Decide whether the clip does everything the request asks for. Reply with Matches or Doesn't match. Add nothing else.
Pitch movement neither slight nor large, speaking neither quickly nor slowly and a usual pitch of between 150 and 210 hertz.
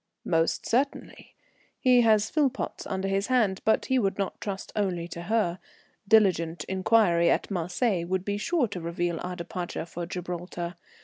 Matches